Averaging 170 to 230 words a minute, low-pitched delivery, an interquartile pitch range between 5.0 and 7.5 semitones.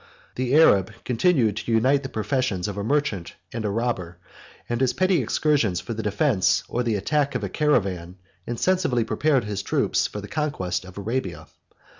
Yes: average, 175 wpm; low, 115 Hz; wide, 5.5 semitones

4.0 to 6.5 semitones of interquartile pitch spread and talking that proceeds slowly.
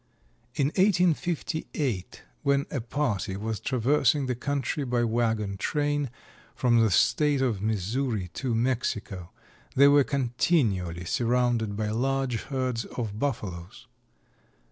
Yes: average, 4.5 semitones; slow, 115 wpm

